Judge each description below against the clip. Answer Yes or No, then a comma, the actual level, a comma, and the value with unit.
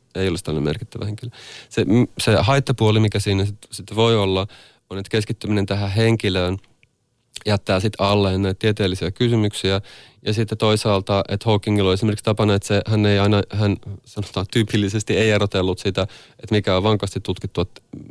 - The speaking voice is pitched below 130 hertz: Yes, low, 105 Hz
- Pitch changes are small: Yes, narrow, 2.1 semitones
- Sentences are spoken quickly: Yes, fast, 165 wpm